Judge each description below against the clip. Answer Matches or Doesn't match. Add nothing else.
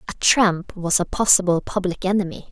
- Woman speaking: Matches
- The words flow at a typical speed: Matches